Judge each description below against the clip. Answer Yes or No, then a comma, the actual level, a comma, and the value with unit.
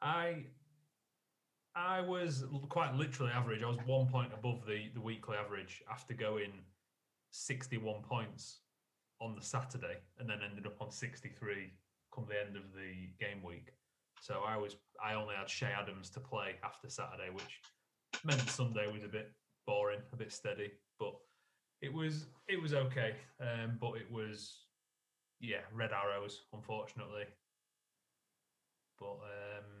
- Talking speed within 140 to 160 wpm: Yes, average, 145 wpm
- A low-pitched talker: Yes, low, 110 Hz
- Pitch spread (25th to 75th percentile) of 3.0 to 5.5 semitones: Yes, average, 4.2 semitones